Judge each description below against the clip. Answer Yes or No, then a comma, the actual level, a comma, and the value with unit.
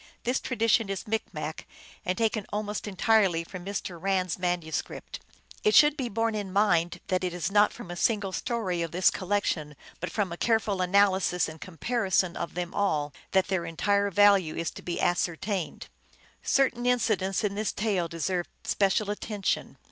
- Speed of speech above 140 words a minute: Yes, average, 170 wpm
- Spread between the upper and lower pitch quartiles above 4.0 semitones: No, average, 3.2 semitones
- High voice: Yes, high, 195 Hz